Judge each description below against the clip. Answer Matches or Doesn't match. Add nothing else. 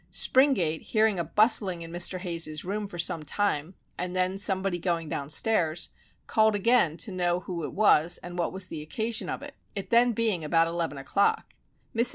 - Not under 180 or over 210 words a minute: Matches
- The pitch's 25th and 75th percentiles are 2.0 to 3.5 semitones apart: Doesn't match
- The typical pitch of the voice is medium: Matches